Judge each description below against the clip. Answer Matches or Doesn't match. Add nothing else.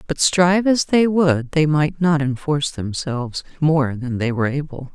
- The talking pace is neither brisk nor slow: Matches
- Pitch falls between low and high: Matches